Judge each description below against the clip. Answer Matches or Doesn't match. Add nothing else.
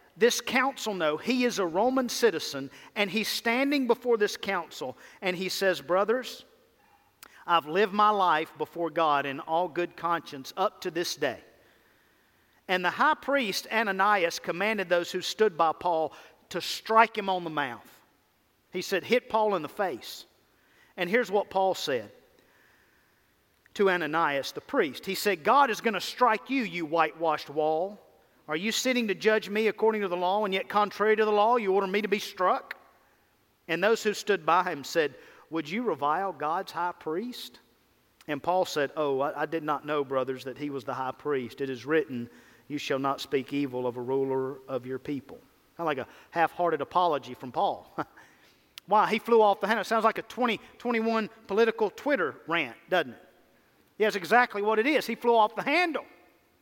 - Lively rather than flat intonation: Matches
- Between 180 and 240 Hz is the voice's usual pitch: Matches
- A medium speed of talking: Matches